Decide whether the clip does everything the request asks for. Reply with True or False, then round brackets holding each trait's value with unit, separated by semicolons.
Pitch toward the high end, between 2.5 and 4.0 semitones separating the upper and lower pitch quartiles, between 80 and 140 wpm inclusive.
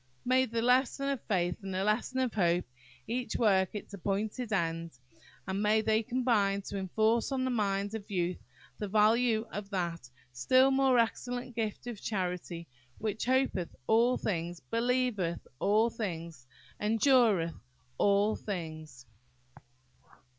False (210 Hz; 4.5 semitones; 135 wpm)